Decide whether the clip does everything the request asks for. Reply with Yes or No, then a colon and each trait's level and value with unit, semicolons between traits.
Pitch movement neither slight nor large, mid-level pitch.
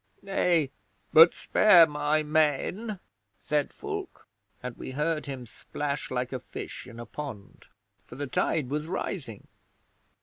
Yes: average, 4.0 semitones; medium, 150 Hz